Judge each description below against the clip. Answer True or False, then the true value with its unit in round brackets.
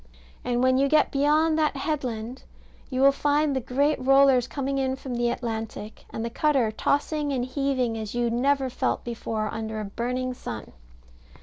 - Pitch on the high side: True (255 Hz)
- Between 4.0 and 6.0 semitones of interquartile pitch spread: False (3.0 semitones)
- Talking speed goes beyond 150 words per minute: True (175 wpm)